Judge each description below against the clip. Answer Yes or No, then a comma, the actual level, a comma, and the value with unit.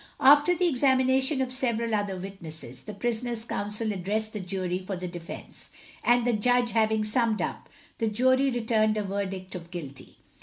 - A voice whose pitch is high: Yes, high, 215 Hz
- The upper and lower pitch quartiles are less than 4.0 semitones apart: No, average, 4.3 semitones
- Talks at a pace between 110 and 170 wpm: Yes, average, 165 wpm